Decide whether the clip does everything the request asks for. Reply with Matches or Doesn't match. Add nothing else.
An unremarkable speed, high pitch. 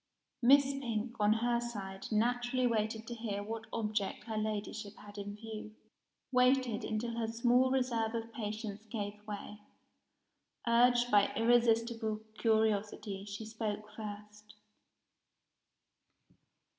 Doesn't match